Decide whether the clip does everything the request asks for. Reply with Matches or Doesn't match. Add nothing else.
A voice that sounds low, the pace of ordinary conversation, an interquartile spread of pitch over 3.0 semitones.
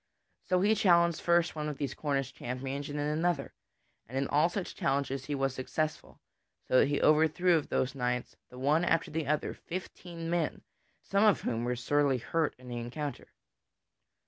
Doesn't match